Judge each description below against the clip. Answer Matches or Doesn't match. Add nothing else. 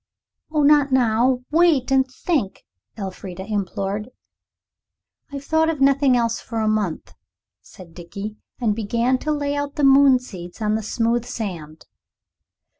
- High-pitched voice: Matches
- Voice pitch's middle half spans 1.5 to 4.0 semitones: Doesn't match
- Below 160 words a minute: Matches